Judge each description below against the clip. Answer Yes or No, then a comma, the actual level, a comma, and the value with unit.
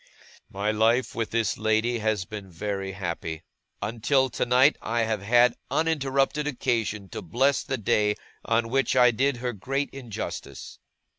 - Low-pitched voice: Yes, low, 115 Hz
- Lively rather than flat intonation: No, average, 3.8 semitones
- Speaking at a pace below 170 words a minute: Yes, average, 145 wpm